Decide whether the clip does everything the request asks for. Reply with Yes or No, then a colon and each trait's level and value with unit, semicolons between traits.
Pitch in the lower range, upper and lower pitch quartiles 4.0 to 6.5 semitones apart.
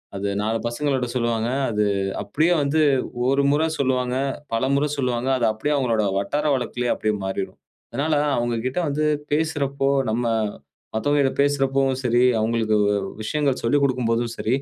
No: low, 125 Hz; average, 3.5 semitones